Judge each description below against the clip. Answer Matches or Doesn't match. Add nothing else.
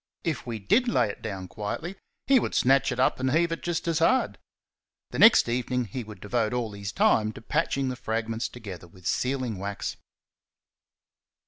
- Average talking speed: Matches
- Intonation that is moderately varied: Doesn't match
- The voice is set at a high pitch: Doesn't match